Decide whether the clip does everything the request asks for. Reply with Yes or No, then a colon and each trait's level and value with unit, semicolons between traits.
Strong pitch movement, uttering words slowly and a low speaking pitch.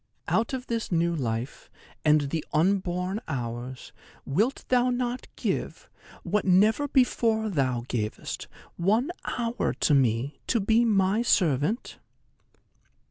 No: wide, 8.6 semitones; slow, 120 wpm; high, 190 Hz